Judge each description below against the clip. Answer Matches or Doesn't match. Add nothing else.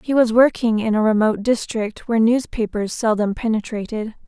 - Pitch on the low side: Doesn't match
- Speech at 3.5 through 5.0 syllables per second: Doesn't match